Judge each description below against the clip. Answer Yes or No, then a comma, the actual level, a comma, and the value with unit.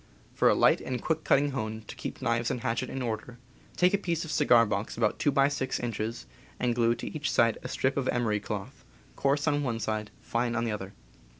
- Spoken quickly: Yes, fast, 230 wpm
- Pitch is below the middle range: Yes, low, 120 Hz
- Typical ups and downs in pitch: Yes, average, 3.6 semitones